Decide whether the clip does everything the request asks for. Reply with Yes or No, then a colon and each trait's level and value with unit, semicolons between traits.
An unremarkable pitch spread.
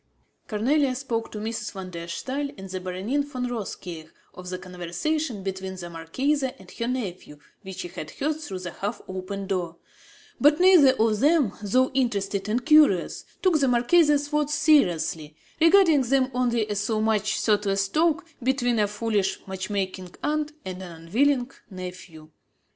No: wide, 6.6 semitones